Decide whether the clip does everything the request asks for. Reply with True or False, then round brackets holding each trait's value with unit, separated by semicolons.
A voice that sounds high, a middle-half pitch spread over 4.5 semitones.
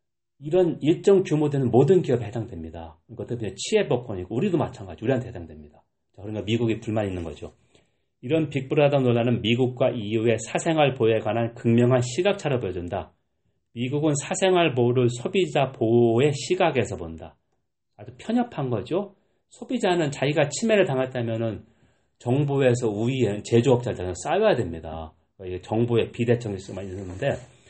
False (120 Hz; 5.3 semitones)